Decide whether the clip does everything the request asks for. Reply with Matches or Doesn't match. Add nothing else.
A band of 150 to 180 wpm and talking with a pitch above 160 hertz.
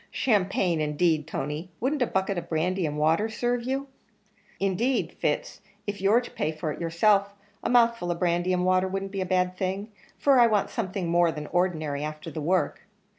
Doesn't match